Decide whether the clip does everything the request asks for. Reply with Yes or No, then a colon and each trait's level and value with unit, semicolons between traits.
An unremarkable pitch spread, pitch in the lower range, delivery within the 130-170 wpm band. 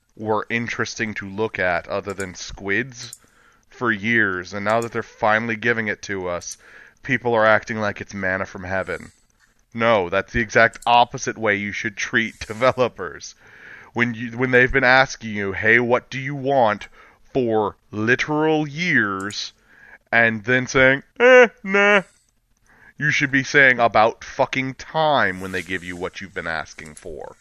Yes: average, 4.1 semitones; low, 115 Hz; average, 160 wpm